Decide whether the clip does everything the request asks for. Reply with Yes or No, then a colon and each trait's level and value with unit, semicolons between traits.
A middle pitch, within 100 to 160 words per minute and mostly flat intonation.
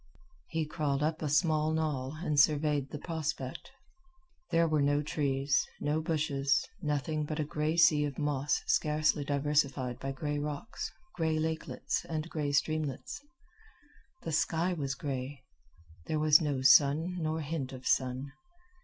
Yes: medium, 150 Hz; average, 145 wpm; narrow, 2.0 semitones